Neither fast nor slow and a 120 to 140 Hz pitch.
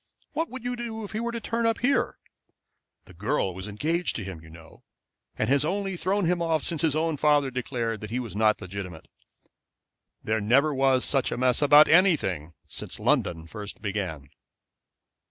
Yes: average, 185 wpm; low, 135 Hz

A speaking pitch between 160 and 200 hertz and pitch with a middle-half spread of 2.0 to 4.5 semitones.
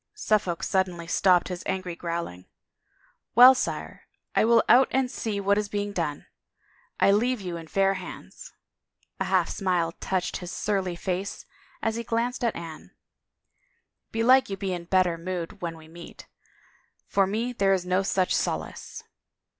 Yes: high, 190 Hz; average, 3.8 semitones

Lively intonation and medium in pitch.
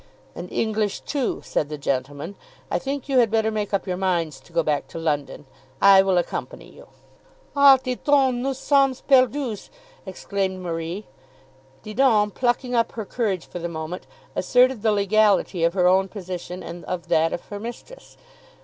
No: wide, 5.9 semitones; high, 200 Hz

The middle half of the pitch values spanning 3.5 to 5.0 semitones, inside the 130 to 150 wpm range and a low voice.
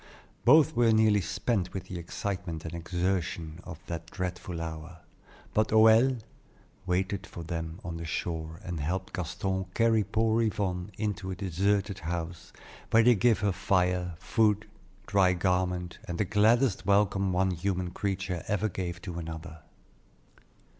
No: average, 3.0 semitones; average, 145 wpm; very low, 95 Hz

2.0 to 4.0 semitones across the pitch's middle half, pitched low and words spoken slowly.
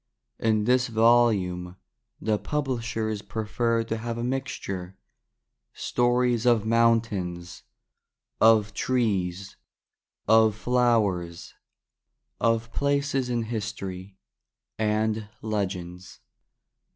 Yes: average, 3.2 semitones; low, 110 Hz; slow, 85 wpm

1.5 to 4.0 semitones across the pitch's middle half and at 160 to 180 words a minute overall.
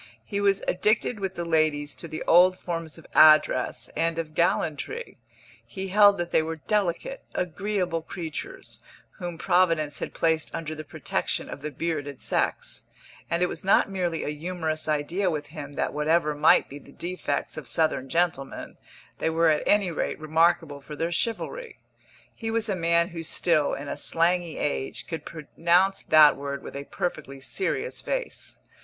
Yes: average, 3.2 semitones; average, 170 wpm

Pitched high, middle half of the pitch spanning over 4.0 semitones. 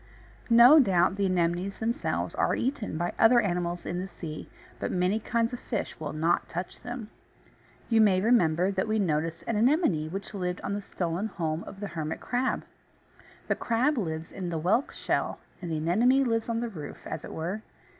Yes: high, 195 Hz; average, 5.0 semitones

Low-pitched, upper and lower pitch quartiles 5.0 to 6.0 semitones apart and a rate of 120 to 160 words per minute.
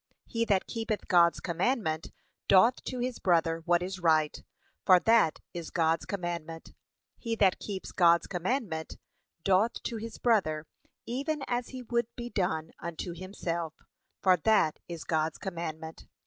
No: medium, 180 Hz; wide, 5.6 semitones; average, 145 wpm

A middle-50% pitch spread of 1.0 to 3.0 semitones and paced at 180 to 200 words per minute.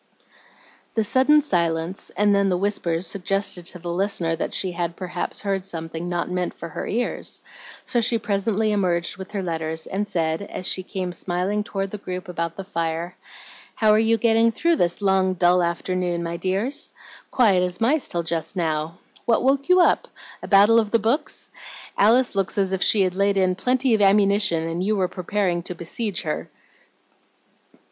No: average, 3.4 semitones; average, 185 wpm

